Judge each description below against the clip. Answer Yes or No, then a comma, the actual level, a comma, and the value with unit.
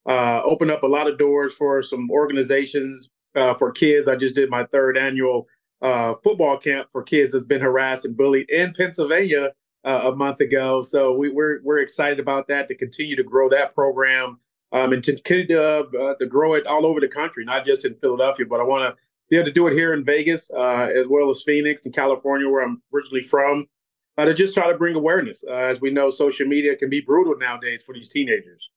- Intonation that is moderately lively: No, narrow, 2.1 semitones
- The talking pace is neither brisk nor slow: No, fast, 225 wpm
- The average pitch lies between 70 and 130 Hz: No, medium, 140 Hz